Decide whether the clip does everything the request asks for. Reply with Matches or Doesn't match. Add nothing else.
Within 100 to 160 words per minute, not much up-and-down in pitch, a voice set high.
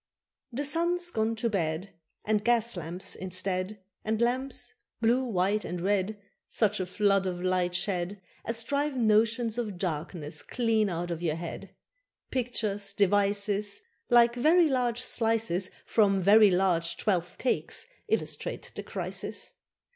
Doesn't match